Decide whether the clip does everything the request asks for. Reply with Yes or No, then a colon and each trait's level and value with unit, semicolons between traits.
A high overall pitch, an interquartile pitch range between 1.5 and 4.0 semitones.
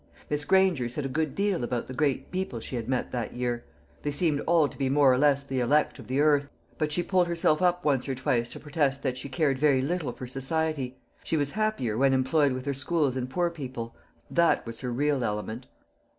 No: medium, 140 Hz; average, 3.4 semitones